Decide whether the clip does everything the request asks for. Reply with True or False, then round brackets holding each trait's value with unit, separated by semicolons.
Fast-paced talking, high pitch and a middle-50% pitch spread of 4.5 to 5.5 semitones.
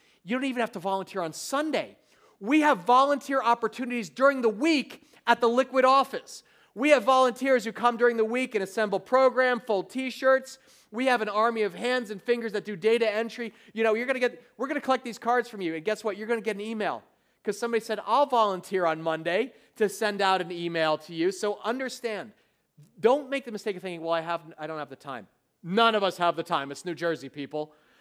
True (230 wpm; 225 Hz; 5.0 semitones)